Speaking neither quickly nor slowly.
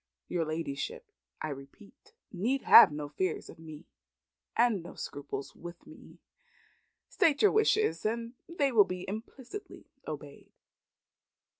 No: slow, 125 wpm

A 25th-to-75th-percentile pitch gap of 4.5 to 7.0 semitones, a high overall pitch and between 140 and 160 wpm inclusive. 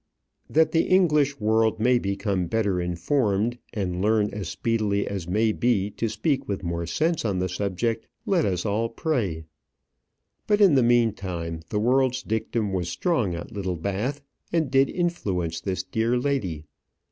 No: average, 5.2 semitones; low, 110 Hz; average, 155 wpm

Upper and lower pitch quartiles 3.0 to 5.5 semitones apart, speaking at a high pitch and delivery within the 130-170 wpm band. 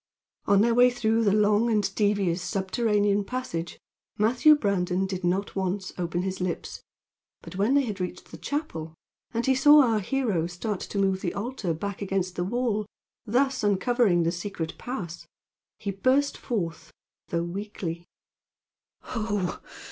Yes: average, 4.3 semitones; high, 200 Hz; average, 150 wpm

